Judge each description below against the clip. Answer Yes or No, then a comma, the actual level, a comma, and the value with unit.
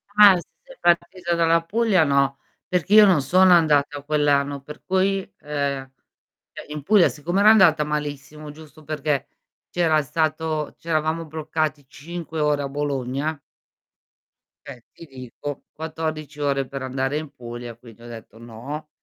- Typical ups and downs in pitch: Yes, average, 3.0 semitones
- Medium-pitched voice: Yes, medium, 150 Hz